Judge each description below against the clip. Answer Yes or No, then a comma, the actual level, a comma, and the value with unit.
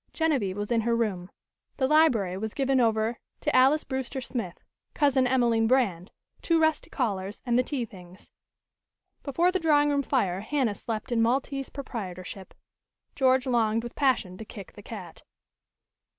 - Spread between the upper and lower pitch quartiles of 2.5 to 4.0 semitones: No, average, 4.7 semitones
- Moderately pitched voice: No, high, 240 Hz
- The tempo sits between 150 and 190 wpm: Yes, average, 155 wpm